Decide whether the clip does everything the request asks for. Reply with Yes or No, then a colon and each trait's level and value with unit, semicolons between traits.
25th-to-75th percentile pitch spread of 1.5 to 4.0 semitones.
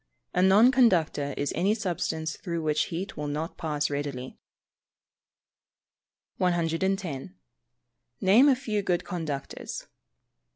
No: average, 4.5 semitones